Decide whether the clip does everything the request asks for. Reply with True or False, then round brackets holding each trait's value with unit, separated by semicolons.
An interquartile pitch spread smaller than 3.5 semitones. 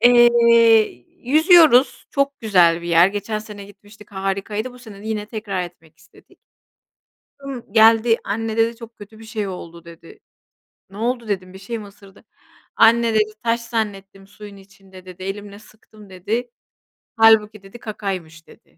True (2.8 semitones)